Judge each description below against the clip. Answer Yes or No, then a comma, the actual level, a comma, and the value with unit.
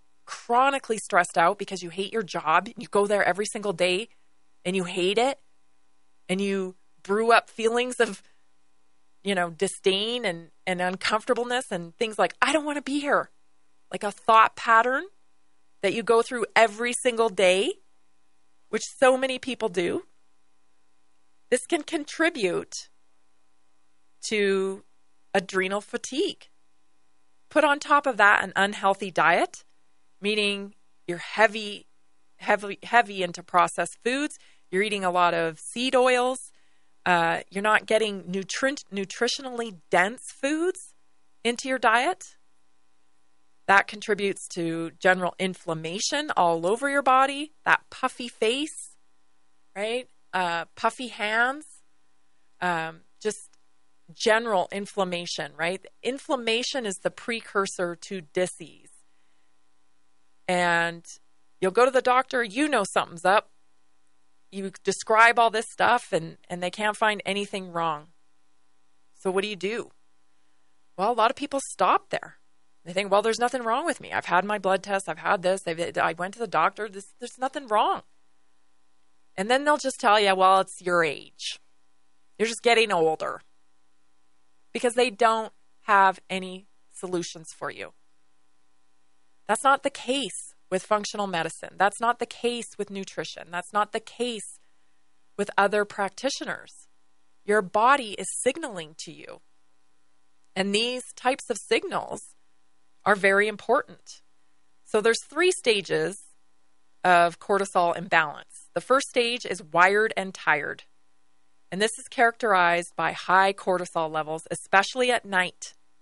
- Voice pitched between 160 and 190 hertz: Yes, medium, 185 Hz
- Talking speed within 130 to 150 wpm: Yes, slow, 135 wpm